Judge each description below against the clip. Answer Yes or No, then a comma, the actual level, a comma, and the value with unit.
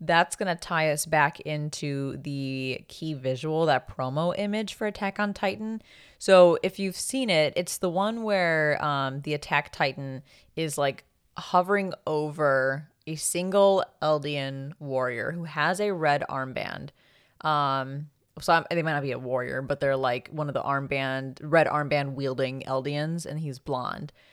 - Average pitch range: Yes, average, 4.2 semitones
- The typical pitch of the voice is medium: Yes, medium, 150 Hz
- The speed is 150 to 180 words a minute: Yes, average, 160 wpm